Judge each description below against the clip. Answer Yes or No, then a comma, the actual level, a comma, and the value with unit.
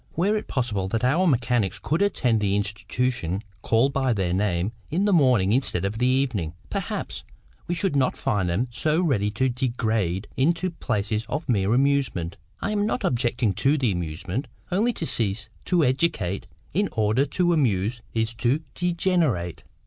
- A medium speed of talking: Yes, average, 165 wpm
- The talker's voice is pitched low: Yes, low, 120 Hz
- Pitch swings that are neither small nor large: No, wide, 6.7 semitones